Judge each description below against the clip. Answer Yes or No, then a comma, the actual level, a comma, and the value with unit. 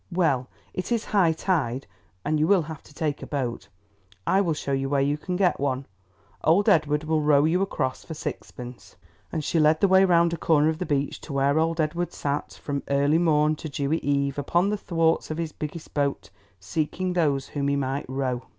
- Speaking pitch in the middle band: Yes, medium, 155 Hz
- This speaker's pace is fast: Yes, fast, 210 wpm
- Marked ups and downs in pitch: No, average, 3.1 semitones